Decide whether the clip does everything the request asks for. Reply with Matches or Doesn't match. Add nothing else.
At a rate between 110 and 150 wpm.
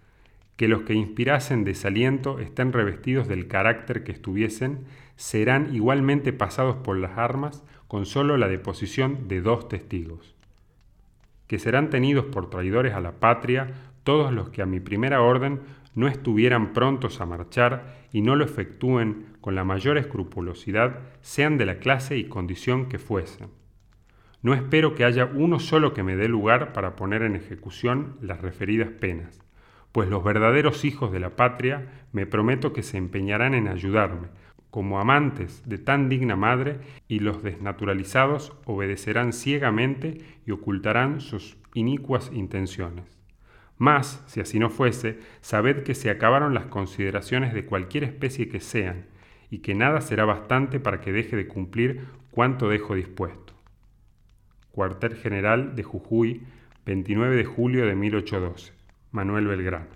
Matches